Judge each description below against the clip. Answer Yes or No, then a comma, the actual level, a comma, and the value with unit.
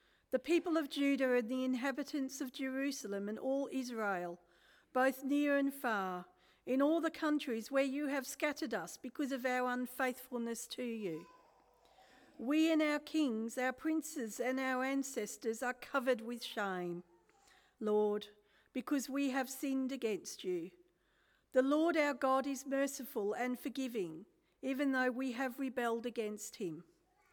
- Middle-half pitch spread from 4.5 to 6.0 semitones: No, average, 3.5 semitones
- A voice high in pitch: Yes, very high, 260 Hz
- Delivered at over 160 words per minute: No, average, 145 wpm